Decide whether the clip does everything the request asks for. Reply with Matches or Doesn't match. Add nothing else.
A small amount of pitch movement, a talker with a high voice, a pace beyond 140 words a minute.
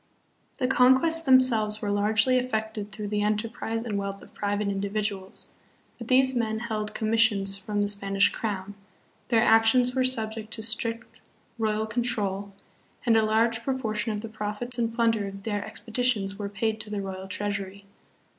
Matches